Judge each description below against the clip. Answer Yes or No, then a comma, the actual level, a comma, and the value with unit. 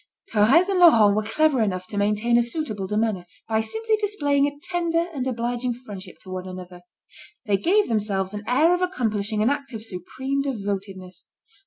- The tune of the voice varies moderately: No, wide, 6.0 semitones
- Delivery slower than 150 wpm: No, average, 170 wpm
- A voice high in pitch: Yes, high, 225 Hz